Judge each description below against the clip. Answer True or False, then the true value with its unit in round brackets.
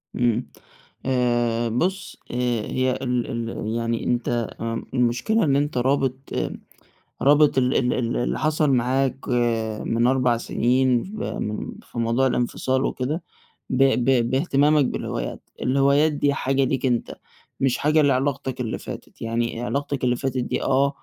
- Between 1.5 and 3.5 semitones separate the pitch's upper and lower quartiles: True (2.4 semitones)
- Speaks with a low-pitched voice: True (130 Hz)